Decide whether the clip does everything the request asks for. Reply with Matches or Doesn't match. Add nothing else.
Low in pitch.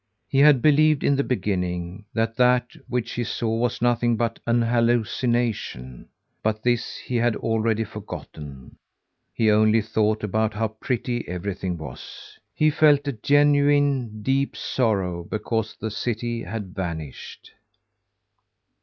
Matches